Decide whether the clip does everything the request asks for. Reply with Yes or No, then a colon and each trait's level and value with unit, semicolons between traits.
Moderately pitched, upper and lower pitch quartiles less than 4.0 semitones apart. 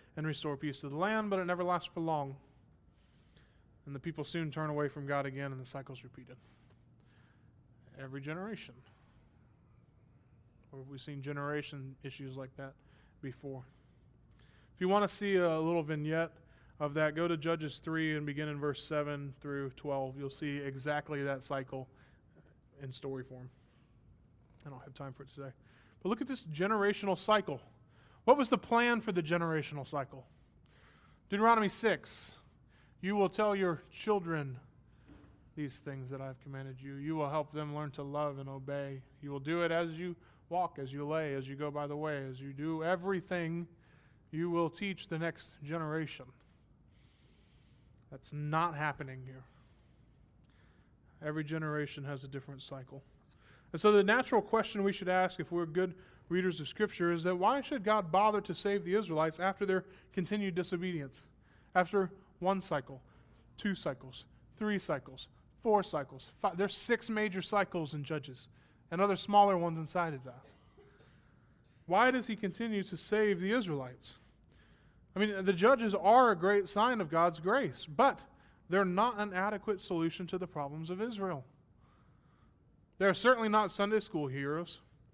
No: medium, 150 Hz; wide, 5.6 semitones